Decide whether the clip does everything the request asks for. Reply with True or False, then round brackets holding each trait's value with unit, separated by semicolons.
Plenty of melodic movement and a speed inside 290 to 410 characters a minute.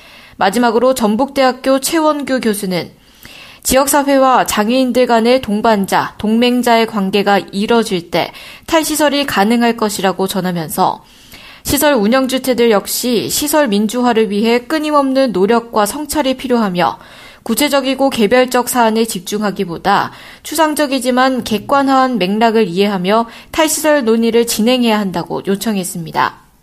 False (4.4 semitones; 315 characters per minute)